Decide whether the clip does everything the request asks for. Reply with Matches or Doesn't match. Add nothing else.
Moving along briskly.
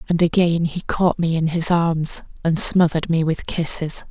Doesn't match